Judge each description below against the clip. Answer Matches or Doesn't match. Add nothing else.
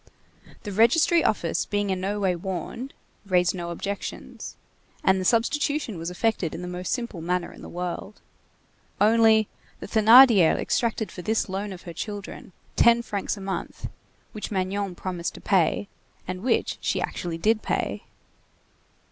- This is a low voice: Doesn't match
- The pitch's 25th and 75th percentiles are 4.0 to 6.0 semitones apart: Doesn't match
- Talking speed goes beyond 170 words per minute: Doesn't match